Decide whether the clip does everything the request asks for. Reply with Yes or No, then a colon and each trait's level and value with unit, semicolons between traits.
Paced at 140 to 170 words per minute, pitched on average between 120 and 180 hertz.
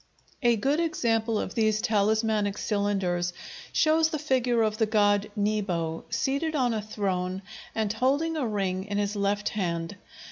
No: average, 155 wpm; high, 215 Hz